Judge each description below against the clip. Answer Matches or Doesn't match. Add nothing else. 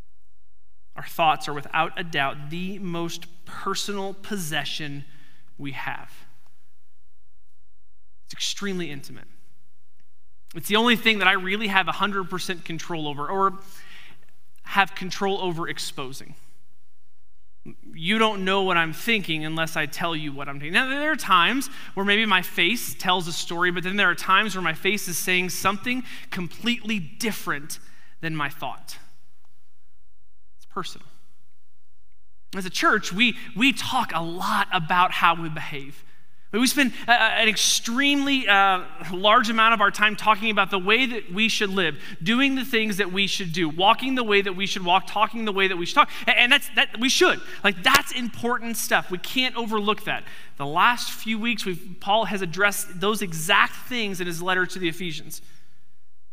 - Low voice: Doesn't match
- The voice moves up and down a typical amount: Doesn't match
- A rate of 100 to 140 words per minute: Doesn't match